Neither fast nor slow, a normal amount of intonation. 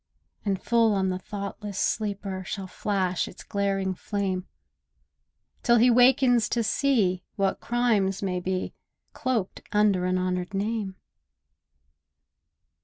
No: slow, 115 wpm; average, 3.0 semitones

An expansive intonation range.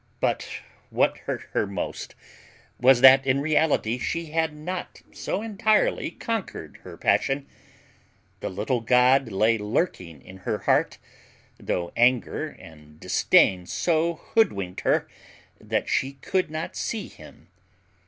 Yes: wide, 7.8 semitones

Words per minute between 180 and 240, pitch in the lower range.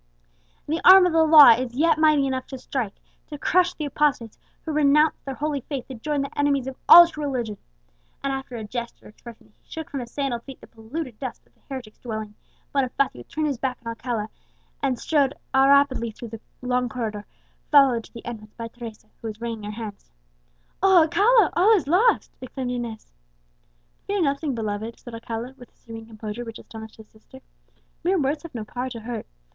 No: average, 200 wpm; very high, 255 Hz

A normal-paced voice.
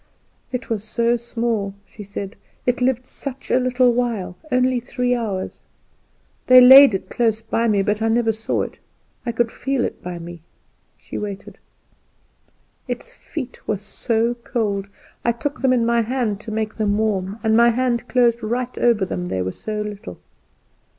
Yes: average, 170 wpm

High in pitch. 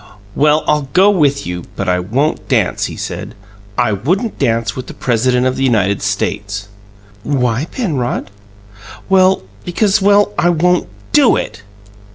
No: low, 135 Hz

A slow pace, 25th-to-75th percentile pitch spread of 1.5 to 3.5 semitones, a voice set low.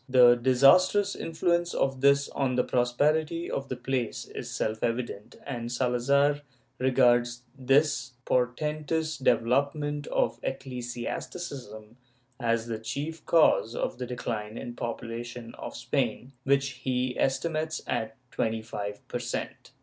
Yes: slow, 125 wpm; average, 3.1 semitones; low, 125 Hz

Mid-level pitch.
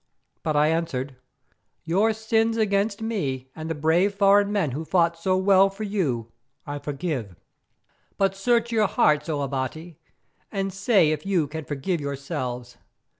Yes: medium, 165 Hz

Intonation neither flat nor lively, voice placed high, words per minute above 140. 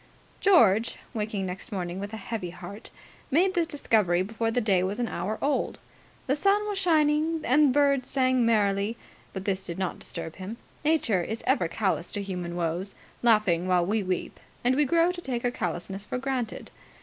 No: wide, 6.4 semitones; high, 220 Hz; average, 185 wpm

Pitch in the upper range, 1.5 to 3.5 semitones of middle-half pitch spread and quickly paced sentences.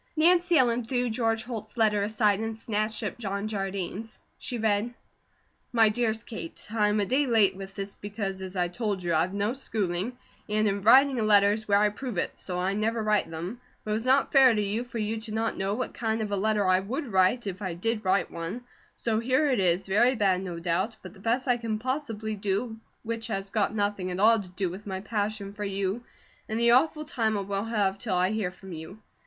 Yes: high, 215 Hz; average, 2.8 semitones; fast, 230 wpm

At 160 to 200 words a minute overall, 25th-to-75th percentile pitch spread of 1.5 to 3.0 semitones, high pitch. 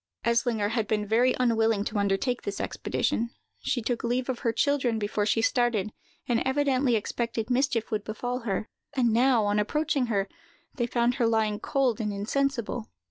Yes: average, 170 wpm; average, 2.7 semitones; high, 235 Hz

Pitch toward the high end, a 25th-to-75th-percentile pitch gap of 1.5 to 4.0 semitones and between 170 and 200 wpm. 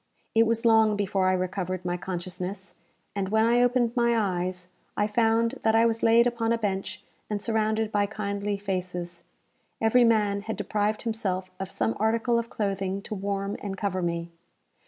Yes: high, 205 Hz; average, 3.1 semitones; average, 175 wpm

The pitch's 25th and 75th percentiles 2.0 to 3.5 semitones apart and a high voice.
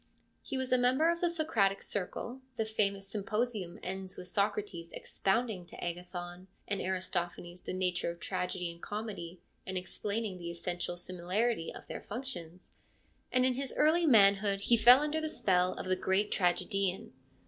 No: average, 4.6 semitones; high, 195 Hz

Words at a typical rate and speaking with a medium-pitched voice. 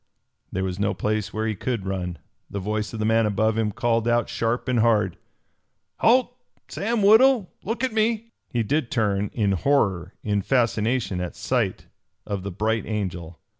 No: average, 170 wpm; low, 110 Hz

